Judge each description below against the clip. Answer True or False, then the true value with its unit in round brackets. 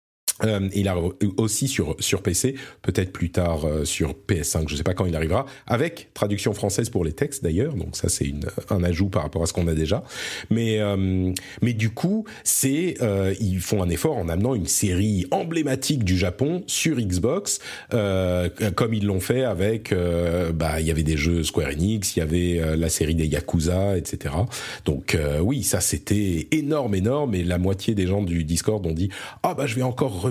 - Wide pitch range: False (4.4 semitones)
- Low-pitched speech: True (95 Hz)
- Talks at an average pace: True (210 wpm)